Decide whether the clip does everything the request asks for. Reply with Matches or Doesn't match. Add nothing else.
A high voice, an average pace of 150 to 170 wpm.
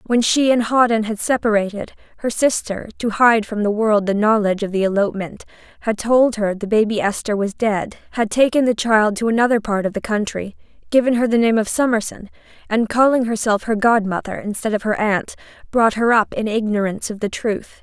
Doesn't match